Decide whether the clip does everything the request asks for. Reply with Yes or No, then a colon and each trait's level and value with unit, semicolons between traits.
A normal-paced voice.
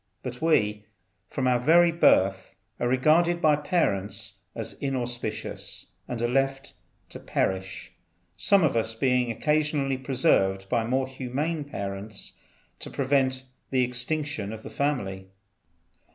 No: slow, 130 wpm